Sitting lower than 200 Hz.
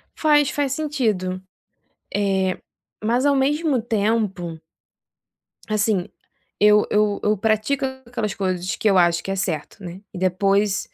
No: high, 210 Hz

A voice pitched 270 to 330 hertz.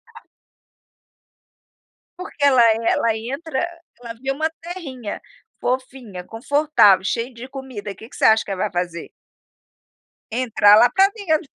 No: very high, 250 Hz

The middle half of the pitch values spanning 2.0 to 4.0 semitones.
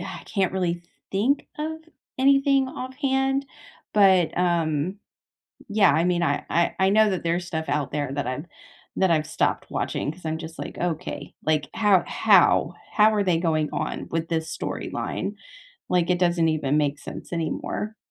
No: average, 4.7 semitones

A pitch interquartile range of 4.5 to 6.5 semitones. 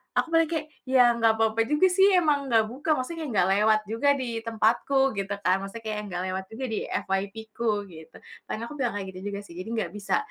Yes: average, 5.2 semitones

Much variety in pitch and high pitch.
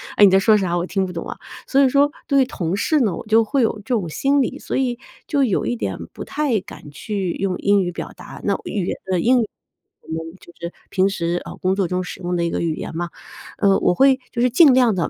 Yes: wide, 6.1 semitones; high, 195 Hz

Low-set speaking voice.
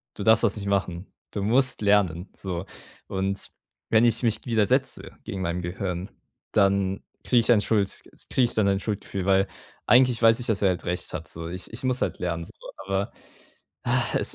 Yes: low, 100 Hz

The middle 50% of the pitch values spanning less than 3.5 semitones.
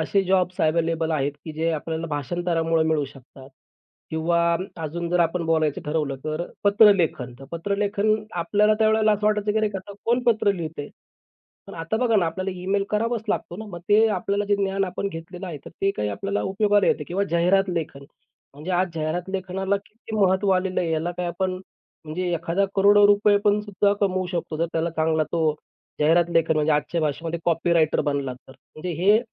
No: average, 3.9 semitones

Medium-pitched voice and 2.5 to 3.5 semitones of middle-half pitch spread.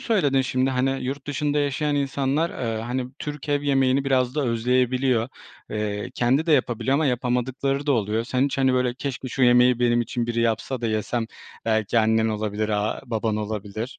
No: low, 125 Hz; average, 3.1 semitones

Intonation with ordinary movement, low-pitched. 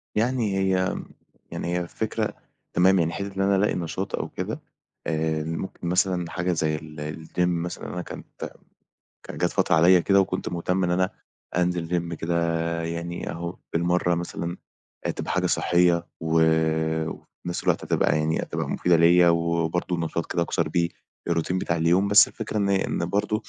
No: narrow, 1.8 semitones; very low, 85 Hz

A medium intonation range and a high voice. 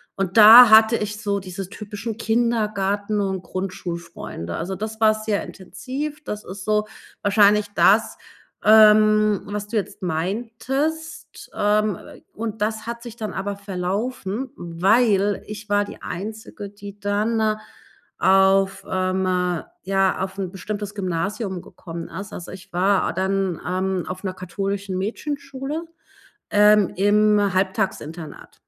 No: narrow, 2.3 semitones; high, 205 Hz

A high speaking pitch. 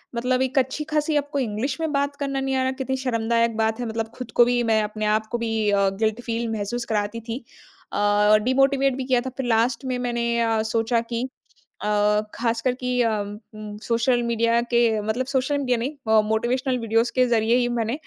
Yes: high, 235 Hz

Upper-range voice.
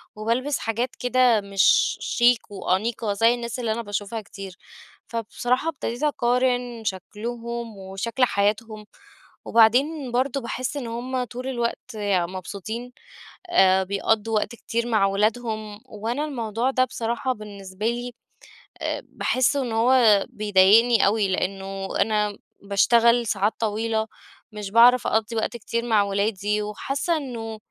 Yes: high, 225 Hz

